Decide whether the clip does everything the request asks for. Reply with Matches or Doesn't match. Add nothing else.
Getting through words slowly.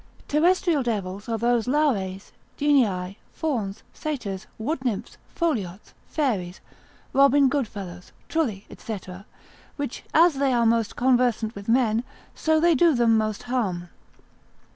Matches